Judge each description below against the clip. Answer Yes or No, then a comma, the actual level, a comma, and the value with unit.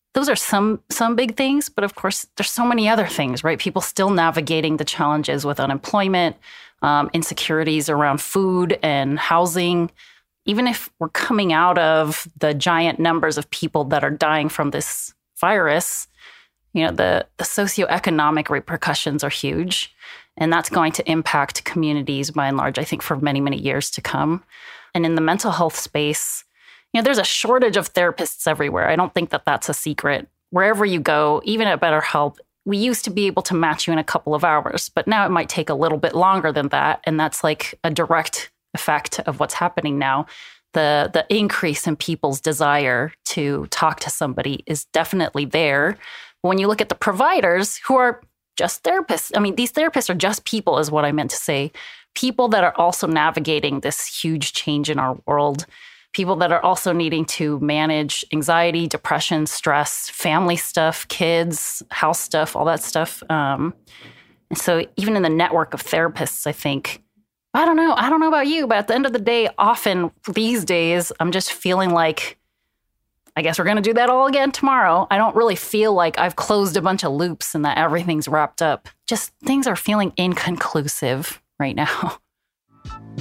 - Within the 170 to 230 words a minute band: Yes, average, 190 wpm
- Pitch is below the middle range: No, medium, 170 Hz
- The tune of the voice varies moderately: Yes, average, 5.0 semitones